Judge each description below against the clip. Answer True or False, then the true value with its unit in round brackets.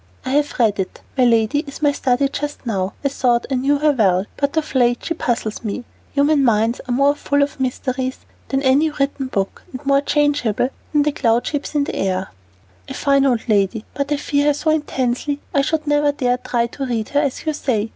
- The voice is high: True (270 Hz)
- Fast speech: True (220 wpm)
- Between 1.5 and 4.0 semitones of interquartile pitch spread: True (3.4 semitones)